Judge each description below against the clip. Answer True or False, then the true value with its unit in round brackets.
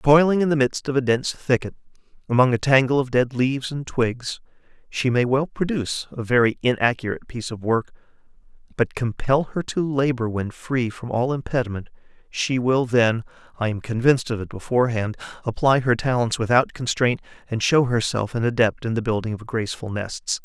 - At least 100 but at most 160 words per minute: False (175 wpm)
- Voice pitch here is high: False (125 Hz)